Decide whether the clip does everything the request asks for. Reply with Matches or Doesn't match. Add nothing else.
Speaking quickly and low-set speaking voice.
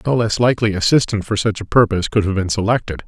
Matches